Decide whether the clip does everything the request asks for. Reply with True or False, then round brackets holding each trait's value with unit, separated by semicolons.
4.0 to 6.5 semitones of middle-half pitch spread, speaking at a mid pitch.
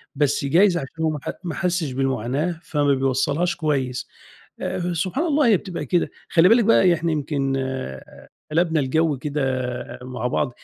True (4.4 semitones; 155 Hz)